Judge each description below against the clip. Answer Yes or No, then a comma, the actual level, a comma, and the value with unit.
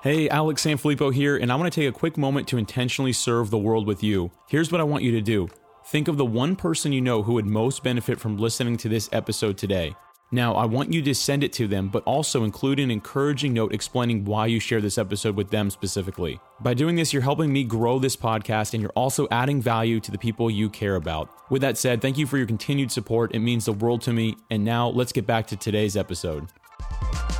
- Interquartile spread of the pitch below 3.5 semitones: No, average, 4.1 semitones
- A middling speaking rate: No, fast, 240 wpm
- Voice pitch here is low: Yes, low, 115 Hz